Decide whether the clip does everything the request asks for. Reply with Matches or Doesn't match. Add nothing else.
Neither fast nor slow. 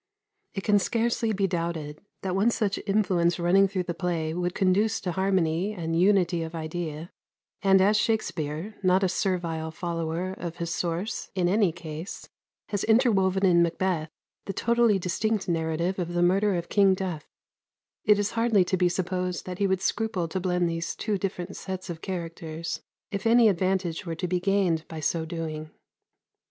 Matches